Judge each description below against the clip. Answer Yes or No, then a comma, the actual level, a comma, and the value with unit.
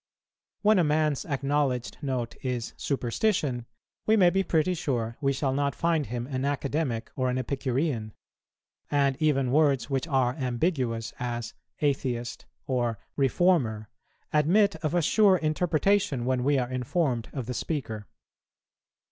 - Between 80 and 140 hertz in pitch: Yes, low, 135 Hz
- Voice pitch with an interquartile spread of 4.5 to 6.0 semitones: No, average, 4.0 semitones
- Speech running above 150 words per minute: No, average, 140 wpm